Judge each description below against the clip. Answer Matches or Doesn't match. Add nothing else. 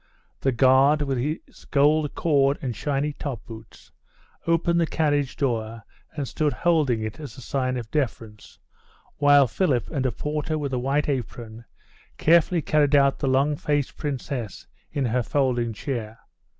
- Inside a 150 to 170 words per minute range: Matches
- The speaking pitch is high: Doesn't match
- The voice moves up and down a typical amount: Matches